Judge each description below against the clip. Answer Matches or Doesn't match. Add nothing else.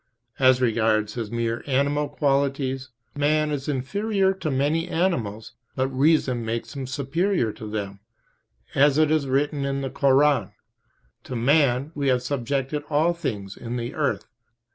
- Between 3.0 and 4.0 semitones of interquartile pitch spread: Matches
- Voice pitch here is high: Doesn't match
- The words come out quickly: Doesn't match